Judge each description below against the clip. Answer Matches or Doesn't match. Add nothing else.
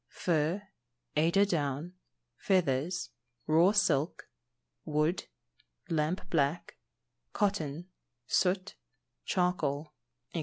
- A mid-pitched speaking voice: Matches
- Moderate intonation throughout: Matches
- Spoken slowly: Matches